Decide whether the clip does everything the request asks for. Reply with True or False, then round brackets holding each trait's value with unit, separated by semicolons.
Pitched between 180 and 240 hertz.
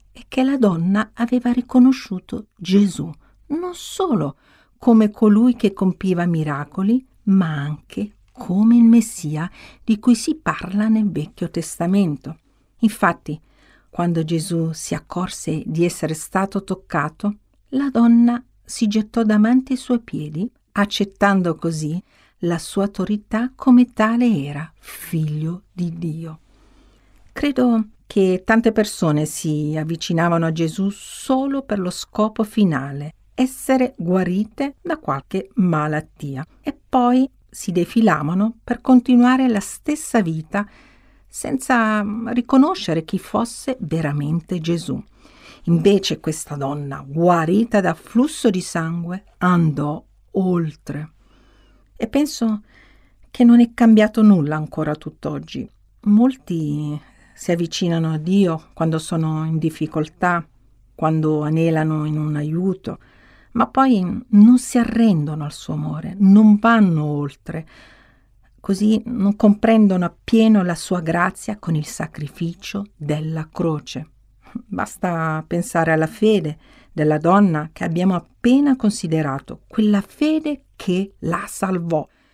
True (185 Hz)